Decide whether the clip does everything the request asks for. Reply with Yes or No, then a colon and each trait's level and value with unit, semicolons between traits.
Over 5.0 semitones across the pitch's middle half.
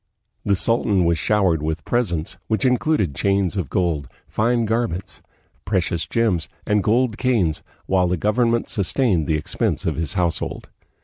Yes: wide, 5.4 semitones